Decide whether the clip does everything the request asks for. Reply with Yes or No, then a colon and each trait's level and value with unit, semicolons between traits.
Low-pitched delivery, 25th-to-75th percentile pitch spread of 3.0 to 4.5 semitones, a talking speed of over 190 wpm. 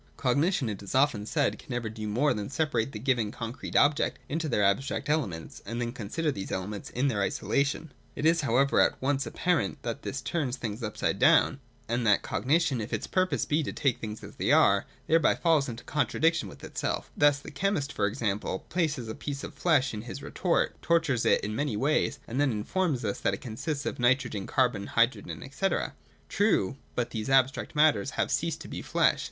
No: low, 130 Hz; average, 5.1 semitones; average, 200 wpm